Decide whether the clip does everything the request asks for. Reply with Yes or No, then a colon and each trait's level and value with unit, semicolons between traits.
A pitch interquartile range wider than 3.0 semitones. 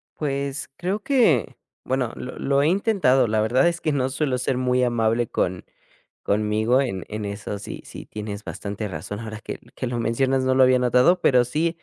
Yes: average, 4.2 semitones